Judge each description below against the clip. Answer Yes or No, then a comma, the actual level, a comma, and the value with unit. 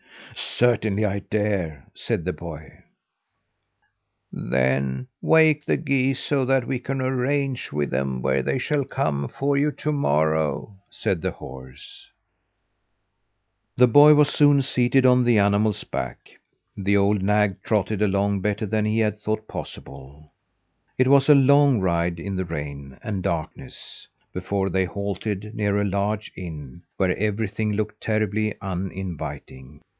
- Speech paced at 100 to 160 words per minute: Yes, average, 140 wpm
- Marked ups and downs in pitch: Yes, wide, 6.3 semitones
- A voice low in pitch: Yes, low, 100 Hz